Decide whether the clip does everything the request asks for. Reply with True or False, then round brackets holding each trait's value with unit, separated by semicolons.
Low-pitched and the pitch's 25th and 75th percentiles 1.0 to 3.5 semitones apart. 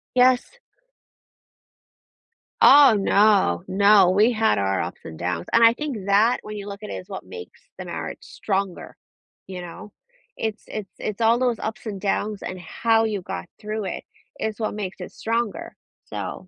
False (210 Hz; 2.9 semitones)